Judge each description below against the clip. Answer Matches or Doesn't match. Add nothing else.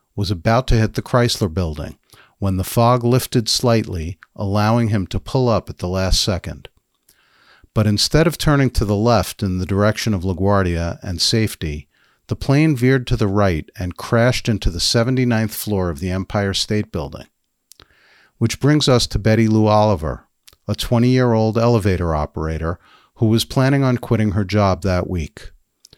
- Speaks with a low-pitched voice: Matches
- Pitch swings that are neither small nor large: Matches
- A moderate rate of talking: Matches